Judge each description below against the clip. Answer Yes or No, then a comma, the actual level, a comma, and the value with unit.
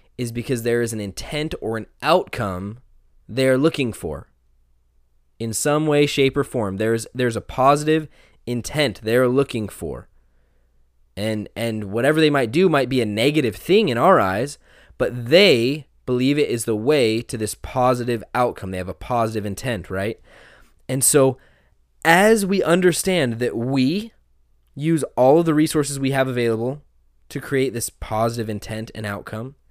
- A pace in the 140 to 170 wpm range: Yes, average, 160 wpm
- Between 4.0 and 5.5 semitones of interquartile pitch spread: Yes, average, 4.9 semitones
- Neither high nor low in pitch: No, low, 120 Hz